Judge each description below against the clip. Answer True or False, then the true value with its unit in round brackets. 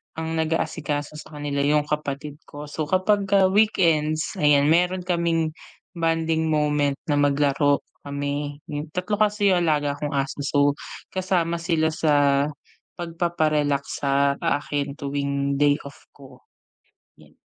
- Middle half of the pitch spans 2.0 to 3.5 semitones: True (2.7 semitones)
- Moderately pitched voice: True (150 Hz)